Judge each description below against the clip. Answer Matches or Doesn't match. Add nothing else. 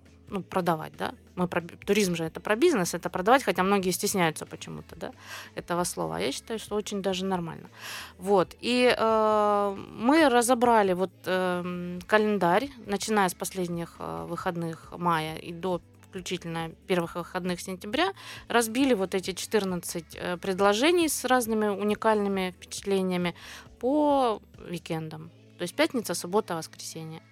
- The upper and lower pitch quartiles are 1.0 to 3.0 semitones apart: Doesn't match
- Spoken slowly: Doesn't match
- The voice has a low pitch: Doesn't match